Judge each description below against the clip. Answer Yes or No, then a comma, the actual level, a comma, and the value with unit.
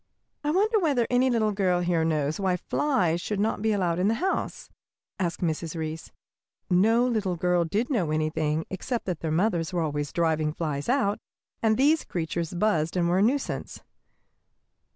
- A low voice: No, medium, 180 Hz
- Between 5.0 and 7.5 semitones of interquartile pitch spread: Yes, wide, 5.5 semitones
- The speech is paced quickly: No, average, 175 wpm